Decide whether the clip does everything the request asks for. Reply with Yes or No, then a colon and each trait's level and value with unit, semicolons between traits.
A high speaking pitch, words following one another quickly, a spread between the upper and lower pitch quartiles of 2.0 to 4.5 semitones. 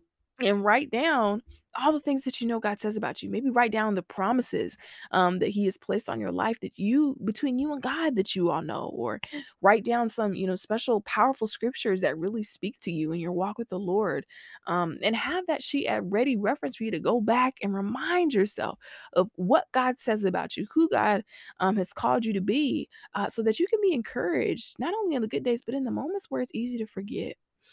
No: high, 225 Hz; fast, 235 wpm; average, 4.9 semitones